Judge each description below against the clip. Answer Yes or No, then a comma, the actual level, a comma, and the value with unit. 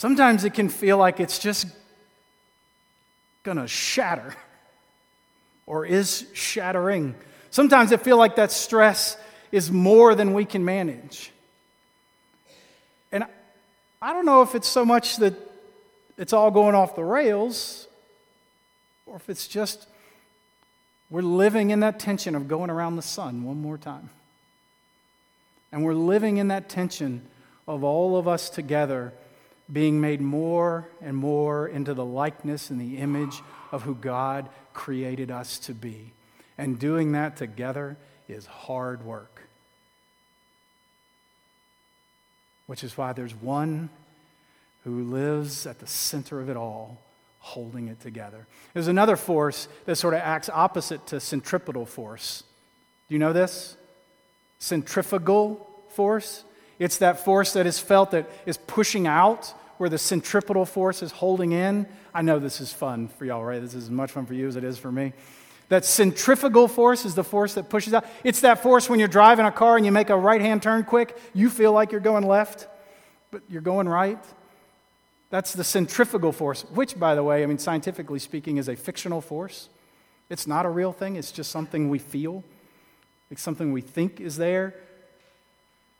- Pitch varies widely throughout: Yes, wide, 6.2 semitones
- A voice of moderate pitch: Yes, medium, 175 Hz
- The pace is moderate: Yes, average, 160 wpm